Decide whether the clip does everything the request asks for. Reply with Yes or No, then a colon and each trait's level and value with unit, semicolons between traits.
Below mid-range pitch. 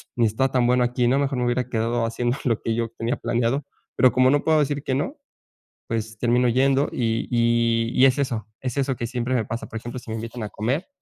Yes: low, 120 Hz